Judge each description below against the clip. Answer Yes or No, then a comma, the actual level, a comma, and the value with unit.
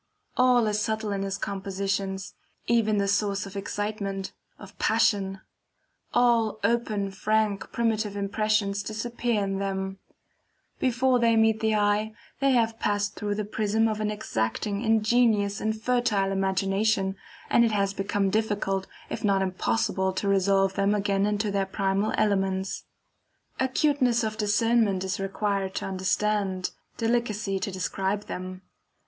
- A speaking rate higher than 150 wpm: No, slow, 135 wpm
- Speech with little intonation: Yes, narrow, 2.0 semitones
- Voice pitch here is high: Yes, high, 205 Hz